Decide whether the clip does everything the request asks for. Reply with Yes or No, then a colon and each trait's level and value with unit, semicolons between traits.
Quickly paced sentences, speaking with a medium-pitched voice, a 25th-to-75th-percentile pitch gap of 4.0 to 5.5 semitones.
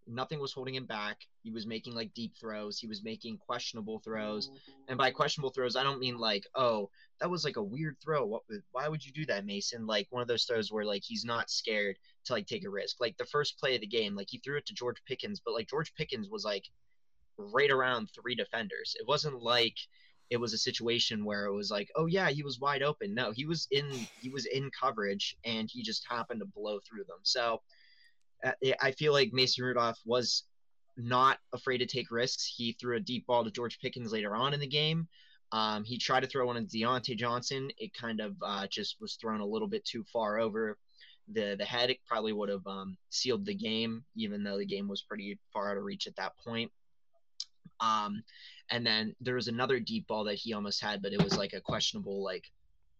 No: fast, 225 wpm; low, 120 Hz; average, 4.4 semitones